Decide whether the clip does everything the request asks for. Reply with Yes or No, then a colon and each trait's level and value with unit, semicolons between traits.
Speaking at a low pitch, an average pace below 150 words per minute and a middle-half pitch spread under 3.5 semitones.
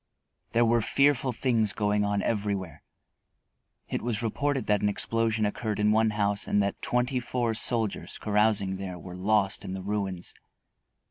No: low, 105 Hz; average, 155 wpm; narrow, 2.4 semitones